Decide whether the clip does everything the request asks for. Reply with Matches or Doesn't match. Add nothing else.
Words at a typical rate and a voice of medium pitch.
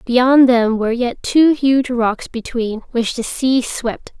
Doesn't match